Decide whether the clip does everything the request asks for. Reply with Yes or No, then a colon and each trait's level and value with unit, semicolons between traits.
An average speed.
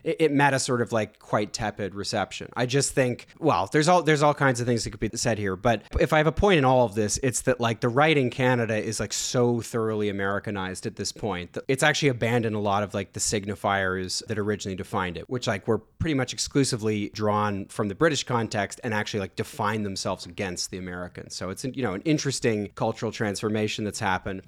No: fast, 230 wpm